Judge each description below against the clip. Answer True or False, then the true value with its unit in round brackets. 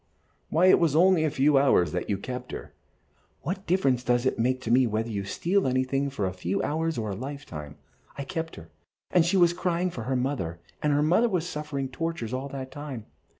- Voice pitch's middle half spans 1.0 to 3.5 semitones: False (5.5 semitones)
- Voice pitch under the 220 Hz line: True (135 Hz)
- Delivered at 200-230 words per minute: True (205 wpm)